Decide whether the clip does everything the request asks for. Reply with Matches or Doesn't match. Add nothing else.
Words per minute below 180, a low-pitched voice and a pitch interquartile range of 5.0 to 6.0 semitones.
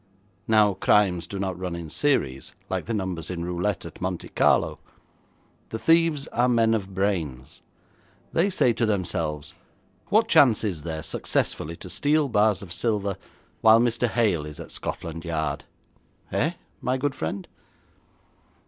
Matches